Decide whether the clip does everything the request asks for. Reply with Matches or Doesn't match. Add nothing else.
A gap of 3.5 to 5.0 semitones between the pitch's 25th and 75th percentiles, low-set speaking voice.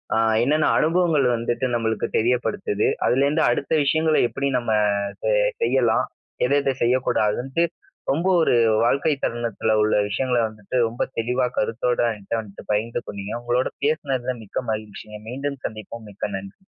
Matches